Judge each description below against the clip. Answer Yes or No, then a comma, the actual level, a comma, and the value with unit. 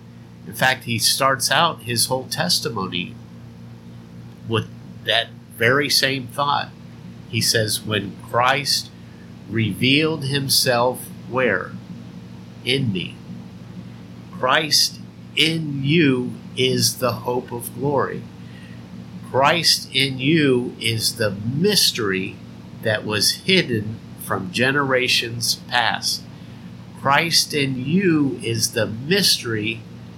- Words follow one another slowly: Yes, slow, 95 wpm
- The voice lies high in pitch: No, low, 110 Hz